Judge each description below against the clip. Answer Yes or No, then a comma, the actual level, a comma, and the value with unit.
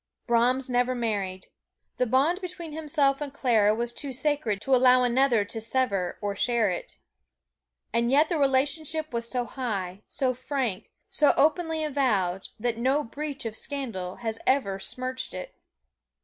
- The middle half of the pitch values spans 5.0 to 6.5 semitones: No, average, 4.0 semitones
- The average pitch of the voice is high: Yes, very high, 255 Hz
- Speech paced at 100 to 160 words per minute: Yes, average, 150 wpm